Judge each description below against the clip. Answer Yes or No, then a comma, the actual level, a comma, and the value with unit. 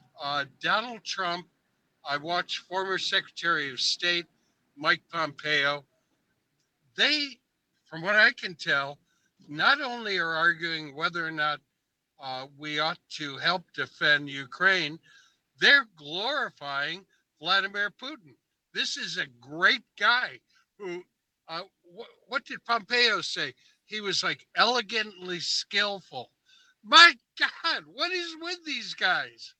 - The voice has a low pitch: No, medium, 180 Hz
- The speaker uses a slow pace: Yes, slow, 120 wpm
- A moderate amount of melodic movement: No, wide, 7.9 semitones